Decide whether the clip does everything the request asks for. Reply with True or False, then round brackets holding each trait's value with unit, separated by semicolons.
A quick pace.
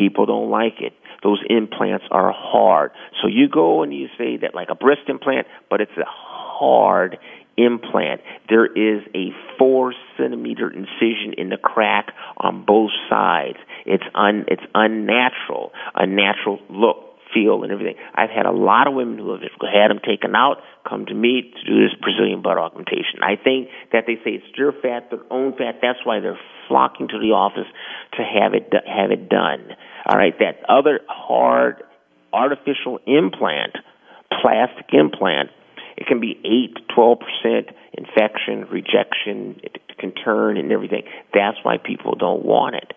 False (165 wpm)